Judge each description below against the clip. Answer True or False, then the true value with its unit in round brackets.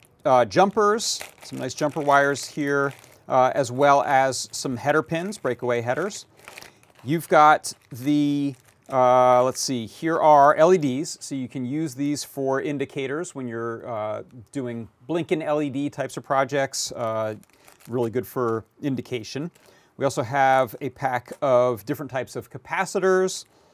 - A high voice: False (135 Hz)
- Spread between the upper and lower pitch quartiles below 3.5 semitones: True (3.0 semitones)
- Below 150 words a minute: True (140 wpm)